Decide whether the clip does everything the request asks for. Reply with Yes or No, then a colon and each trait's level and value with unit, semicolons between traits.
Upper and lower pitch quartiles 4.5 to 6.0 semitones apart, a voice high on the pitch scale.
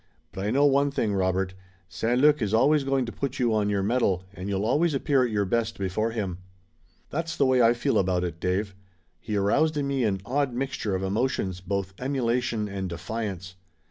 No: wide, 5.5 semitones; low, 110 Hz